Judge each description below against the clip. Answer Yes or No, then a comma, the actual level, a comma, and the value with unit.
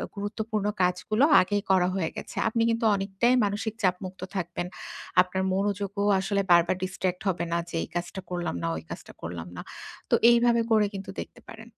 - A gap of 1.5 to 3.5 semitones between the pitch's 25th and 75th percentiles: Yes, narrow, 2.6 semitones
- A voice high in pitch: Yes, high, 195 Hz